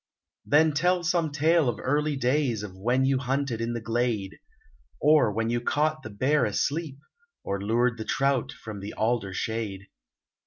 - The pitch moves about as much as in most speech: Yes, average, 5.0 semitones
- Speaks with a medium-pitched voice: No, low, 125 Hz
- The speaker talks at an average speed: Yes, average, 165 wpm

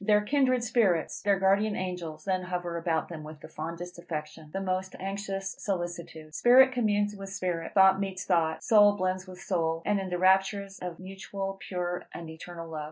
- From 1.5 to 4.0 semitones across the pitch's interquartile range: Yes, average, 2.7 semitones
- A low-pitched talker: No, medium, 185 Hz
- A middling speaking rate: Yes, average, 180 wpm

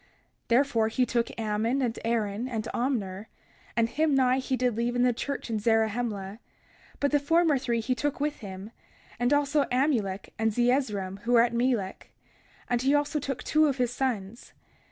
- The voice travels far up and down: No, average, 3.5 semitones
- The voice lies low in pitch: No, high, 240 Hz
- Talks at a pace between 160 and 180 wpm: Yes, average, 175 wpm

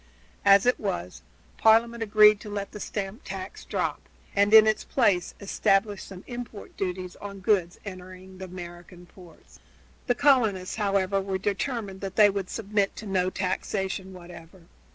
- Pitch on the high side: Yes, high, 195 Hz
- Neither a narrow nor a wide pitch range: No, narrow, 2.3 semitones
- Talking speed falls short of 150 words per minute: No, average, 155 wpm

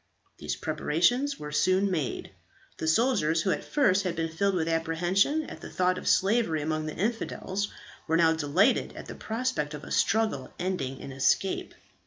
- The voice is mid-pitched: Yes, medium, 175 Hz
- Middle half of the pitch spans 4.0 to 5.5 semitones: Yes, average, 4.5 semitones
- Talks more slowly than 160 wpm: No, average, 175 wpm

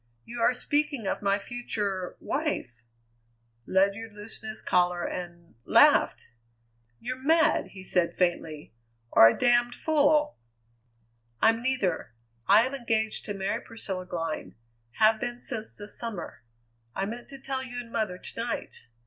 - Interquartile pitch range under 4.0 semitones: No, average, 4.6 semitones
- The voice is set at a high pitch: Yes, high, 220 Hz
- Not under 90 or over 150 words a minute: Yes, average, 140 wpm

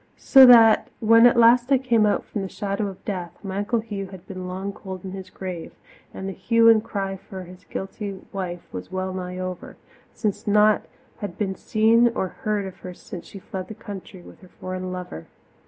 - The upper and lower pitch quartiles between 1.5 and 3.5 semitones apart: Yes, average, 2.7 semitones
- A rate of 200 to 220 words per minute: Yes, fast, 205 wpm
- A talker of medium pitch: No, high, 195 Hz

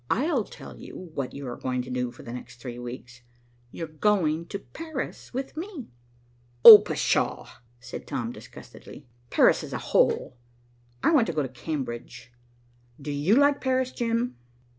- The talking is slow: No, average, 160 wpm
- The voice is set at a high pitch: No, medium, 155 Hz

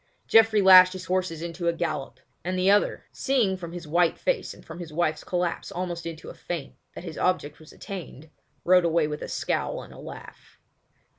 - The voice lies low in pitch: No, medium, 175 Hz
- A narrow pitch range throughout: Yes, narrow, 2.2 semitones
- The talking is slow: No, average, 200 wpm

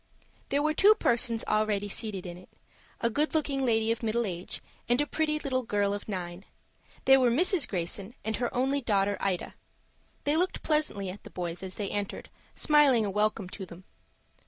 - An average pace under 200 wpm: Yes, average, 180 wpm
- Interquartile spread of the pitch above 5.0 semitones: Yes, wide, 5.6 semitones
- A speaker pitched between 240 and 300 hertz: No, high, 220 Hz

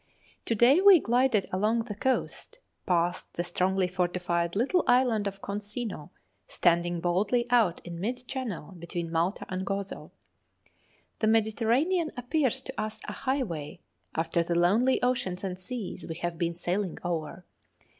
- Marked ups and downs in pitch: Yes, wide, 5.8 semitones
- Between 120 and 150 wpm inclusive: Yes, average, 145 wpm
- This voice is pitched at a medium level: No, high, 200 Hz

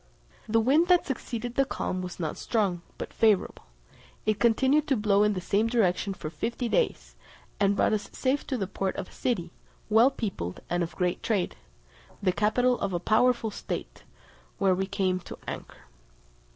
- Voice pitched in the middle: No, high, 210 Hz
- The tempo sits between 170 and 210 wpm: Yes, average, 180 wpm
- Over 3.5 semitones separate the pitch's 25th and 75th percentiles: Yes, average, 4.6 semitones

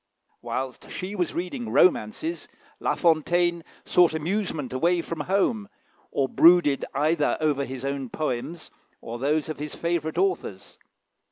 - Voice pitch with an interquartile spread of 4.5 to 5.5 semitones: No, average, 4.0 semitones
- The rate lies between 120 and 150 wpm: Yes, slow, 135 wpm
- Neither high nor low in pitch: Yes, medium, 160 Hz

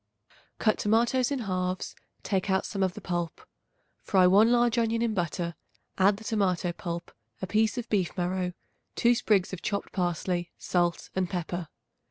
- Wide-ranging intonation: No, average, 3.7 semitones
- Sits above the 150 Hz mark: Yes, high, 190 Hz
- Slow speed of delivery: No, average, 165 wpm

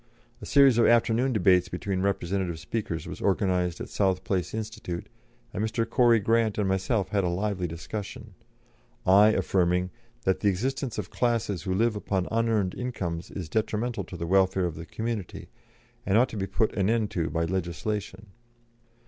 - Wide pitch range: No, average, 3.5 semitones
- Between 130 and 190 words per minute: Yes, average, 170 wpm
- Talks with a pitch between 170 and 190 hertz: No, low, 100 Hz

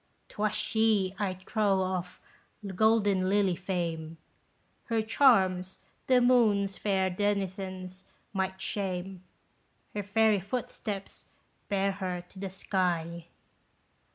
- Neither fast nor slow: No, slow, 100 wpm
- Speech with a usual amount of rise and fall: No, narrow, 1.9 semitones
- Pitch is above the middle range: Yes, high, 195 Hz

